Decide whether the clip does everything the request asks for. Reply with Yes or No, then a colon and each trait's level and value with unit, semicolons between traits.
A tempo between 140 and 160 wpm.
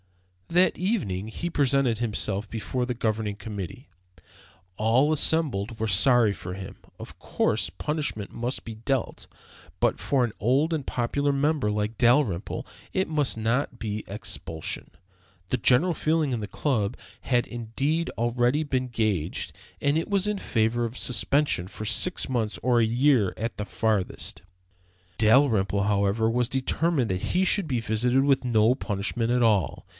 Yes: average, 150 wpm